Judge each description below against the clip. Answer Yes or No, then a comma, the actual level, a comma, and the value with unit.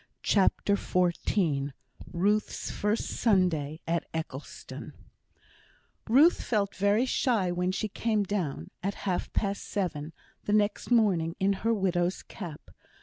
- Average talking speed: No, slow, 120 wpm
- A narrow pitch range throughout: No, average, 3.5 semitones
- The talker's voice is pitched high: Yes, high, 195 Hz